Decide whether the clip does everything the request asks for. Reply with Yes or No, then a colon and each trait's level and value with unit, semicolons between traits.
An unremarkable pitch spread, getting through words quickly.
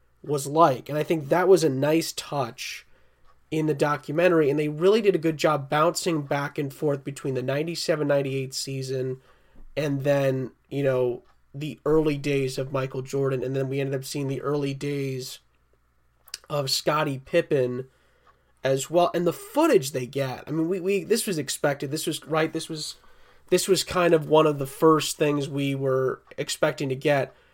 No: average, 3.1 semitones; average, 185 wpm